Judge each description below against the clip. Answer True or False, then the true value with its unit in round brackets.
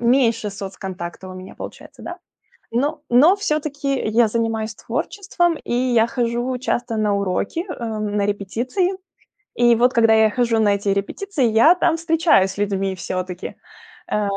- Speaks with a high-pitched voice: True (230 Hz)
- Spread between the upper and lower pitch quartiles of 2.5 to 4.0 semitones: False (4.7 semitones)